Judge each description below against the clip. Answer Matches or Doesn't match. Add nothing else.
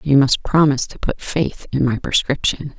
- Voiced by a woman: Matches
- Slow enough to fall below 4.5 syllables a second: Doesn't match